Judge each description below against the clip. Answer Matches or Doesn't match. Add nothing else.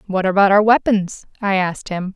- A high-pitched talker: Matches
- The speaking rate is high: Doesn't match